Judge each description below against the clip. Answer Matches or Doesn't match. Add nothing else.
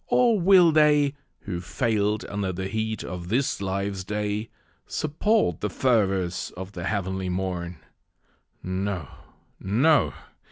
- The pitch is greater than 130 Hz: Doesn't match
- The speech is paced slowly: Matches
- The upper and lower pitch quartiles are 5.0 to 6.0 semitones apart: Matches